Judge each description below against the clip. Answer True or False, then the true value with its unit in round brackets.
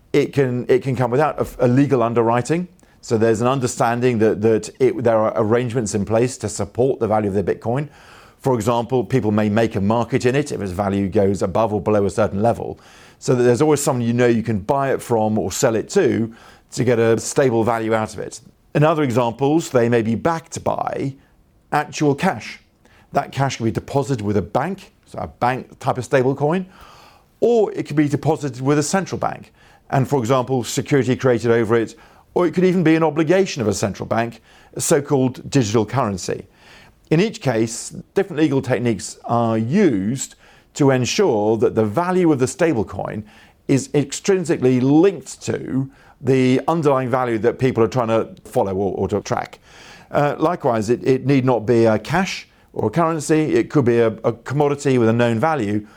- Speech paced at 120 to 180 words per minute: False (195 wpm)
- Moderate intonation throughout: True (4.2 semitones)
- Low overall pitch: True (125 Hz)